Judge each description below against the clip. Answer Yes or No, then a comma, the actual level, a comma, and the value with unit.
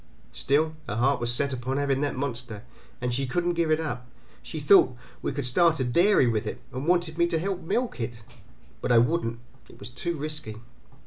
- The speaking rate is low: No, fast, 205 wpm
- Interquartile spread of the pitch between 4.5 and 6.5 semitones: Yes, average, 4.8 semitones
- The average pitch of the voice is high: No, medium, 140 Hz